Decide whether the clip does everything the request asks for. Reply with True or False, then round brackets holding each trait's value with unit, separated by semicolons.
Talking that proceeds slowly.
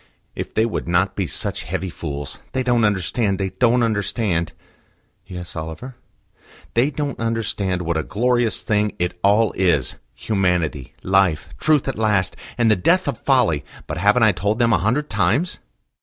False (165 wpm)